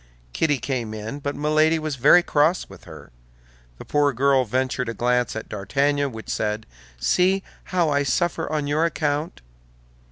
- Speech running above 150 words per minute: Yes, average, 160 wpm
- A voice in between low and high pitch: Yes, medium, 145 Hz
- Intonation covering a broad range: No, average, 3.9 semitones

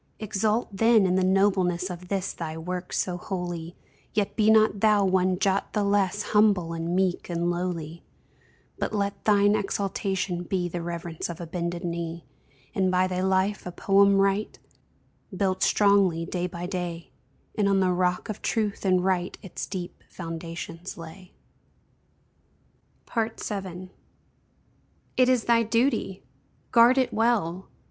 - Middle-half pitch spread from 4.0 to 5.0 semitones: No, narrow, 2.5 semitones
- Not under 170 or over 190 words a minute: No, average, 145 wpm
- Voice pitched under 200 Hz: Yes, medium, 185 Hz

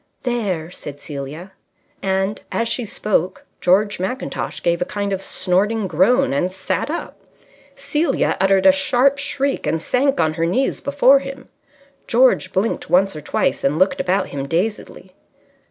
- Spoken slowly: No, average, 155 wpm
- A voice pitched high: Yes, high, 195 Hz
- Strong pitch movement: Yes, wide, 6.2 semitones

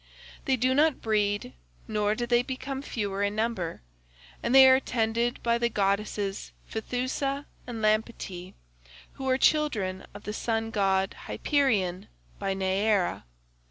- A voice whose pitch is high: Yes, high, 220 Hz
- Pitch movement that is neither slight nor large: Yes, average, 4.2 semitones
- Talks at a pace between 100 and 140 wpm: Yes, slow, 135 wpm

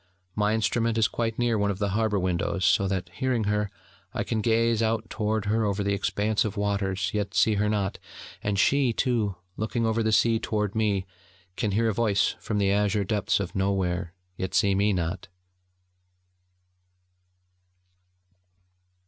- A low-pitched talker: Yes, low, 105 Hz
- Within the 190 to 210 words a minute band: No, average, 165 wpm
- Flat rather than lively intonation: Yes, narrow, 2.1 semitones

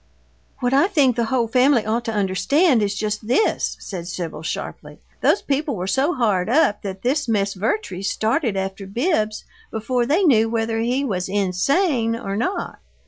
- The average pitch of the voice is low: No, high, 225 Hz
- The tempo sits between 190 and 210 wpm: No, average, 170 wpm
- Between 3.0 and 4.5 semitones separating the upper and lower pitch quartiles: No, average, 5.2 semitones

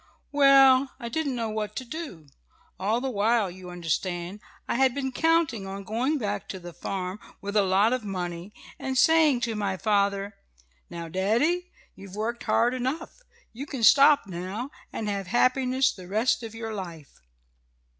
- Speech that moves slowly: No, average, 165 wpm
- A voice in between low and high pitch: No, high, 220 Hz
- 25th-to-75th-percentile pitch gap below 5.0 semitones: No, average, 5.3 semitones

